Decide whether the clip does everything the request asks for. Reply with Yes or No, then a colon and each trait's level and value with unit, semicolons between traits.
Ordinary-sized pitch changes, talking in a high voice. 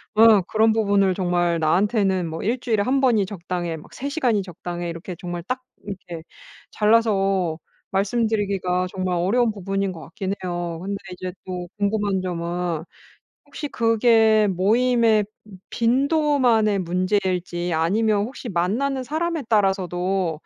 Yes: average, 4.1 semitones; high, 195 Hz